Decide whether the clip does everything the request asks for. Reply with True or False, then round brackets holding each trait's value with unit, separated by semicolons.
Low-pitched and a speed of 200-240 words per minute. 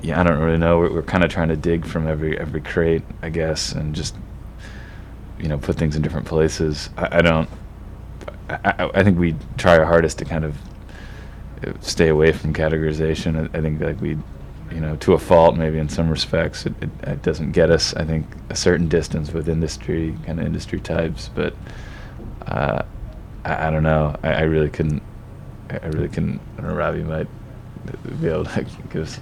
True (80 Hz; 205 wpm)